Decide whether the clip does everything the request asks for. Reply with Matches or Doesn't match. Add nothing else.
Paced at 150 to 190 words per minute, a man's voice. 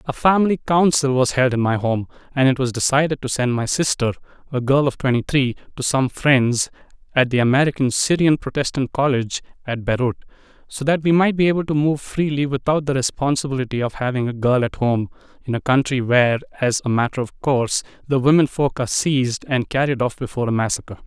Doesn't match